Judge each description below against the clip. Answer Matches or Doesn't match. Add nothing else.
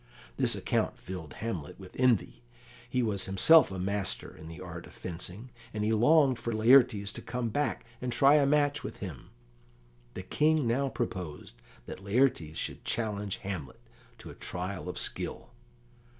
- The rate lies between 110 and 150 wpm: Doesn't match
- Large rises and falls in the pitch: Matches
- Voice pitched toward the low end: Matches